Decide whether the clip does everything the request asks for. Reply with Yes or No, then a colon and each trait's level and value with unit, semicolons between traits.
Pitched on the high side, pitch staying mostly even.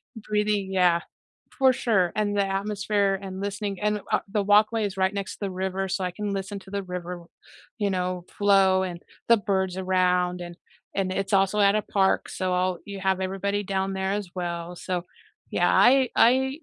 Yes: high, 195 Hz; narrow, 1.8 semitones